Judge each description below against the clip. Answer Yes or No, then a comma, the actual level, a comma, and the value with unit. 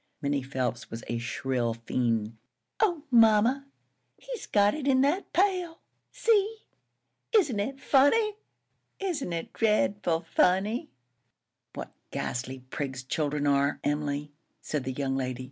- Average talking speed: No, slow, 125 wpm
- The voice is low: No, medium, 170 Hz